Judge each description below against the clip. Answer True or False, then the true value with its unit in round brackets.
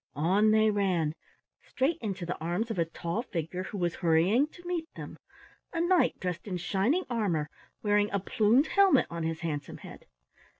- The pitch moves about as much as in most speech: False (6.0 semitones)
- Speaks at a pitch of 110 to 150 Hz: False (200 Hz)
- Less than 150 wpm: False (175 wpm)